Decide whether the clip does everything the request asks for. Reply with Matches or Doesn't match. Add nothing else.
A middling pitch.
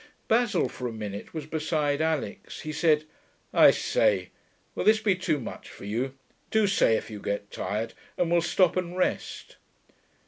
Matches